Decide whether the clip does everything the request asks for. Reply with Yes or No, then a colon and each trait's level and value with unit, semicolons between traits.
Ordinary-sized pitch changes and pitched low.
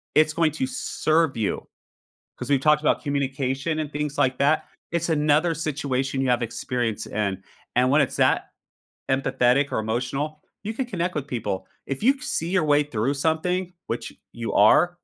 No: average, 3.8 semitones; medium, 145 Hz